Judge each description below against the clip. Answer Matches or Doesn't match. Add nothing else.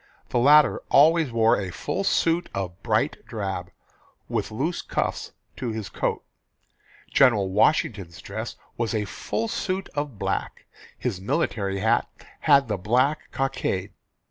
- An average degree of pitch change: Doesn't match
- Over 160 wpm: Doesn't match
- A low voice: Matches